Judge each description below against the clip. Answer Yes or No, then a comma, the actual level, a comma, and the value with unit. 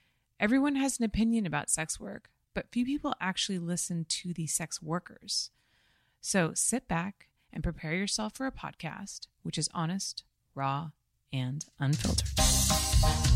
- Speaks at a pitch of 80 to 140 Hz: No, medium, 170 Hz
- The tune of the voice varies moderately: No, wide, 6.7 semitones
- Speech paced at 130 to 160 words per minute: Yes, average, 140 wpm